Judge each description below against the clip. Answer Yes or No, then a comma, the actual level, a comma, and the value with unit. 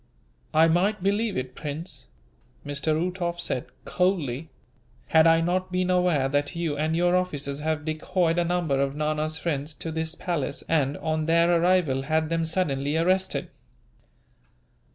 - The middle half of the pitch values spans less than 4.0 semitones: Yes, average, 3.2 semitones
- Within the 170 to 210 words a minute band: No, average, 150 wpm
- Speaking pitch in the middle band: Yes, medium, 160 Hz